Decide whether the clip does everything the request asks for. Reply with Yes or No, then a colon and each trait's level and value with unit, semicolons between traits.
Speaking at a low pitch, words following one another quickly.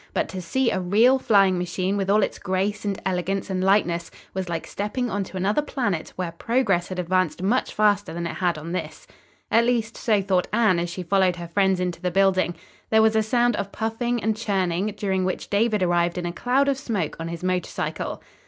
No: high, 195 Hz; fast, 215 wpm